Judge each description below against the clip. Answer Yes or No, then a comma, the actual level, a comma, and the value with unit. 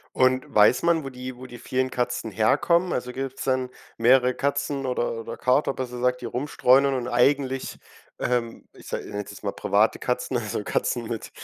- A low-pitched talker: Yes, low, 125 Hz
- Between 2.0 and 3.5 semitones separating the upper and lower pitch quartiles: No, narrow, 1.6 semitones